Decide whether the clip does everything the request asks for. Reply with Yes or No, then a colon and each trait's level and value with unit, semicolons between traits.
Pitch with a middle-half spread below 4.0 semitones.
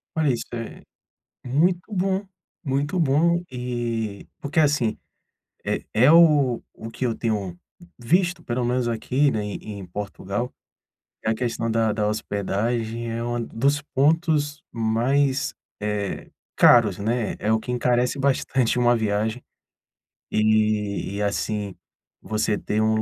No: average, 4.3 semitones